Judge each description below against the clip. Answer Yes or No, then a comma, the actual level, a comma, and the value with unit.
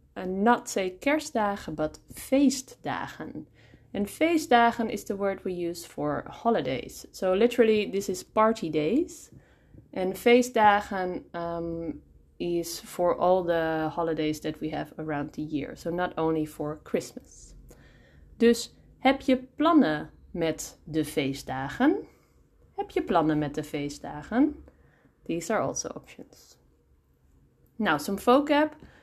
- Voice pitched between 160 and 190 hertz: Yes, medium, 185 Hz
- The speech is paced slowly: Yes, slow, 125 wpm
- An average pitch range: No, wide, 7.3 semitones